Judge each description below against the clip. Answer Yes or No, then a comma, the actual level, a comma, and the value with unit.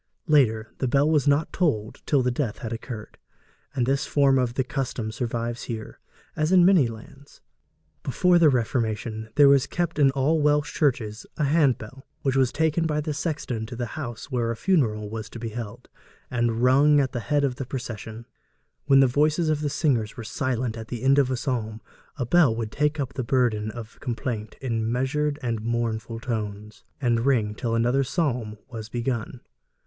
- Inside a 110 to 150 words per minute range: No, average, 185 wpm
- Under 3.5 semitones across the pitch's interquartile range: No, average, 3.9 semitones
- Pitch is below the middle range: Yes, low, 125 Hz